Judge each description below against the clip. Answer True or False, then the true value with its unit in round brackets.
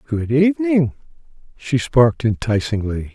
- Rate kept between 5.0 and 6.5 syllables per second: False (4.5 syllables/s)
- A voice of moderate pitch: False (130 Hz)